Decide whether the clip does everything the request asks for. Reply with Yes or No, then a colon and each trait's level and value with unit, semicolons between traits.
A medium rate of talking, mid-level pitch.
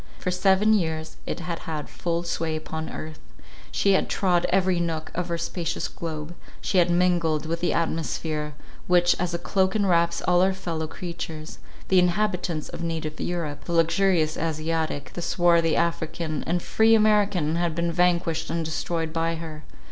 Yes: average, 155 wpm; medium, 170 Hz